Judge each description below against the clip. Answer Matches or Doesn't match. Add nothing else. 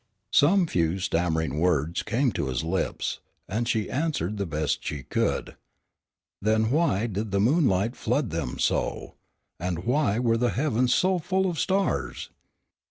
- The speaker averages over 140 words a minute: Matches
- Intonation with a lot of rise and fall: Matches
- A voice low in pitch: Matches